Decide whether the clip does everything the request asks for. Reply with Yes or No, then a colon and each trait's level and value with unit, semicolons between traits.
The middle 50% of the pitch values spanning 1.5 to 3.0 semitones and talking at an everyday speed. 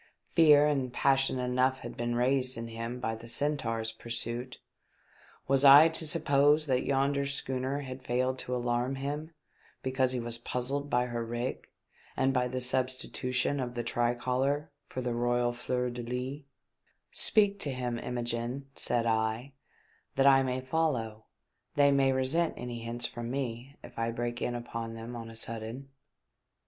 Yes: narrow, 2.4 semitones; average, 160 wpm